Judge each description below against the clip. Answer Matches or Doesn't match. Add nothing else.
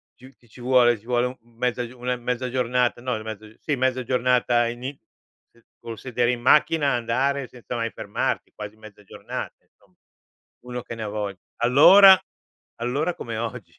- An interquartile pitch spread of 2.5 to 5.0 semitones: Doesn't match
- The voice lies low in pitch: Matches